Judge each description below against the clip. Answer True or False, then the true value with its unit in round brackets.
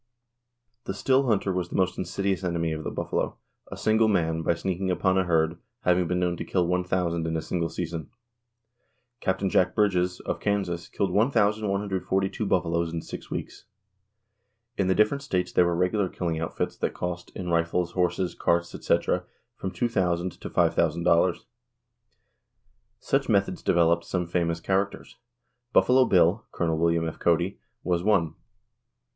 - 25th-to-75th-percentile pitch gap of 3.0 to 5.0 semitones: False (2.4 semitones)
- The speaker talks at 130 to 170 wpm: True (155 wpm)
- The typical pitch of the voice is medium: False (90 Hz)